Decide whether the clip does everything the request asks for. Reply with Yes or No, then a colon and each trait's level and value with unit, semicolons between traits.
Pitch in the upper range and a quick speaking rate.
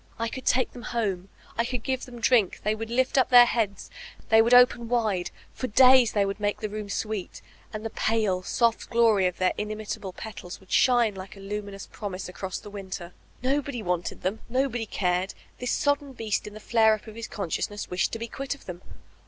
Yes: high, 215 Hz; fast, 210 wpm